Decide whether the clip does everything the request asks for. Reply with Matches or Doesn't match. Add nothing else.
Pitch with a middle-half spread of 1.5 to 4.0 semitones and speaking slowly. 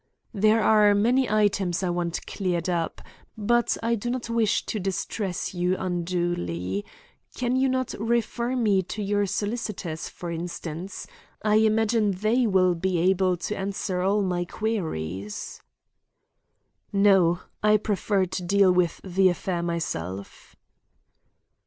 Matches